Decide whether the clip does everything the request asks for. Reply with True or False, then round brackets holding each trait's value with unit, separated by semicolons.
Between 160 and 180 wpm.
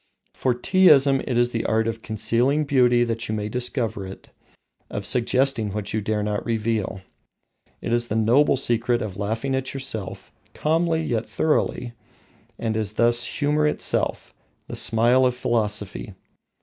False (150 wpm)